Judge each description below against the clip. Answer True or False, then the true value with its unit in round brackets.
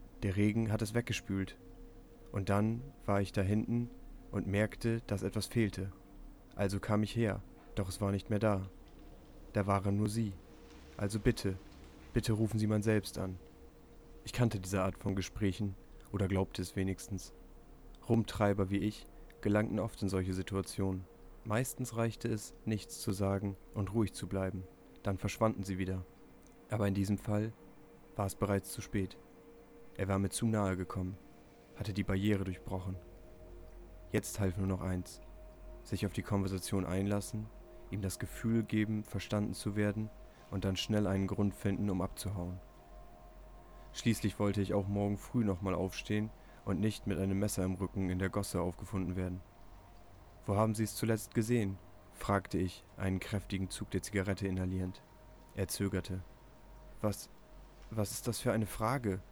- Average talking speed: True (160 wpm)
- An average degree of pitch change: False (2.3 semitones)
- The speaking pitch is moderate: False (100 Hz)